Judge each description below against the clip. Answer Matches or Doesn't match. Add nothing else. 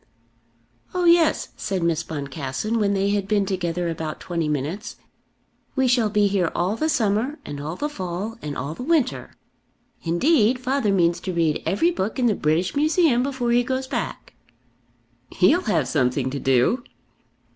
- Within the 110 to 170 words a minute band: Matches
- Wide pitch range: Matches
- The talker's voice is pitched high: Matches